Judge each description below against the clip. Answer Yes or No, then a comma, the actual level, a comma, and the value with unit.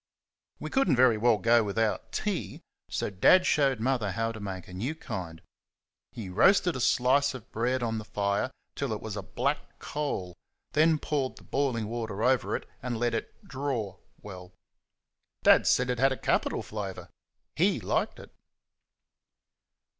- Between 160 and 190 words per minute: Yes, average, 170 wpm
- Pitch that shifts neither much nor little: Yes, average, 4.3 semitones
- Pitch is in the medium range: No, low, 115 Hz